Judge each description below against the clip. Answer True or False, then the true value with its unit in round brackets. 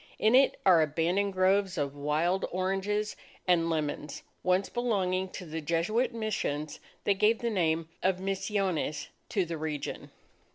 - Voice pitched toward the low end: False (185 Hz)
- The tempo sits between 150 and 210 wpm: False (140 wpm)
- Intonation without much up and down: False (3.8 semitones)